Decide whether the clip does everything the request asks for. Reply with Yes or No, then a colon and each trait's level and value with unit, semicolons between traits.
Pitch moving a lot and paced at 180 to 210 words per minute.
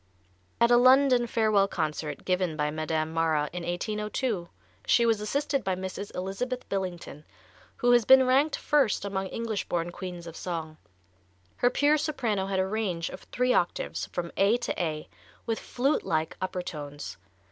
No: wide, 6.1 semitones; average, 160 wpm